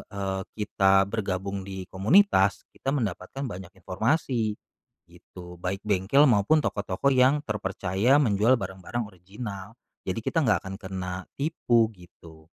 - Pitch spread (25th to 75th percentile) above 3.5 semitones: Yes, average, 4.0 semitones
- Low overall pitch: Yes, low, 100 Hz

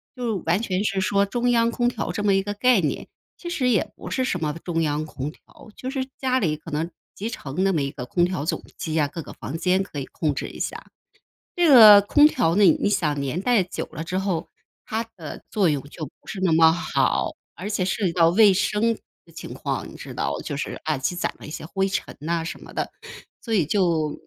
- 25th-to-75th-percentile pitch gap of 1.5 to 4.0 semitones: No, average, 5.0 semitones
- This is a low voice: No, medium, 185 Hz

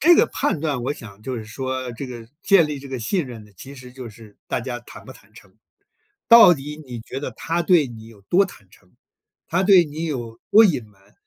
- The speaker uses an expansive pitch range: Yes, wide, 5.7 semitones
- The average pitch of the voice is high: No, low, 130 Hz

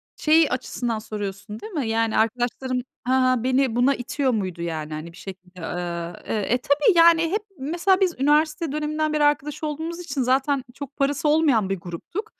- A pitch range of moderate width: No, wide, 5.9 semitones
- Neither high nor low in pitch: No, very high, 260 Hz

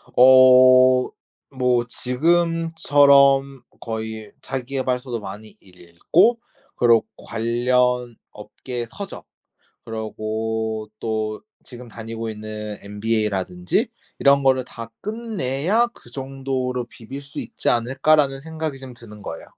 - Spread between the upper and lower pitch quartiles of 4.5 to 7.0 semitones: No, average, 3.6 semitones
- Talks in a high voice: No, low, 125 Hz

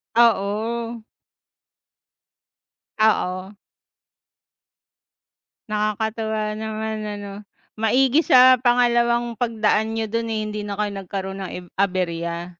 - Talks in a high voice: Yes, high, 220 Hz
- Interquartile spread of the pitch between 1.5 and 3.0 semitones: Yes, narrow, 2.6 semitones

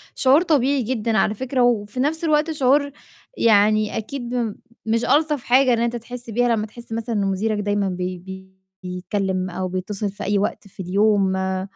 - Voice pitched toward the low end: No, high, 220 Hz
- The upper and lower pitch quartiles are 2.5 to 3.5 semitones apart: No, average, 4.2 semitones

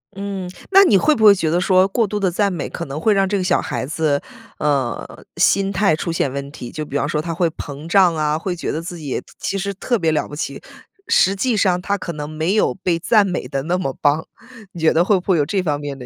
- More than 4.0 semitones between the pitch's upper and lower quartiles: Yes, average, 4.5 semitones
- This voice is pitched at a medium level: Yes, medium, 175 Hz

